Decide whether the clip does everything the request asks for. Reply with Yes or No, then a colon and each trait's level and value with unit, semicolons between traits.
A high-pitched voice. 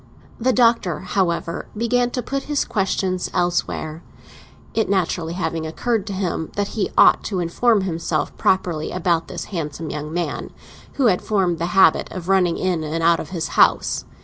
No: medium, 180 Hz